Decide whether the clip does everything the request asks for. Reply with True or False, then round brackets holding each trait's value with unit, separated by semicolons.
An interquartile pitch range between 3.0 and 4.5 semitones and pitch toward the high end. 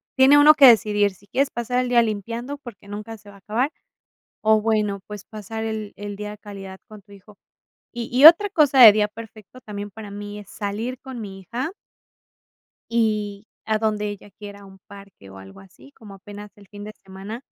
False (2.4 semitones; 210 Hz)